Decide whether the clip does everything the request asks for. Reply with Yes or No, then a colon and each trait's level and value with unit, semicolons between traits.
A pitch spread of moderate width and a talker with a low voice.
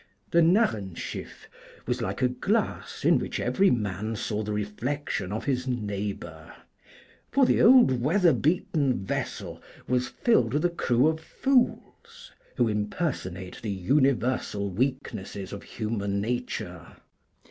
No: wide, 6.7 semitones; low, 120 Hz